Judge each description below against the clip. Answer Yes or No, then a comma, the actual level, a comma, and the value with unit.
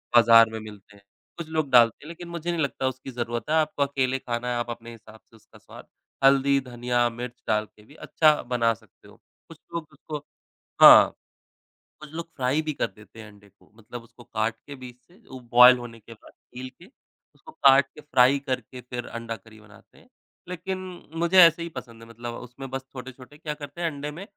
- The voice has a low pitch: Yes, low, 125 Hz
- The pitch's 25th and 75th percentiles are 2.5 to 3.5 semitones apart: No, average, 4.2 semitones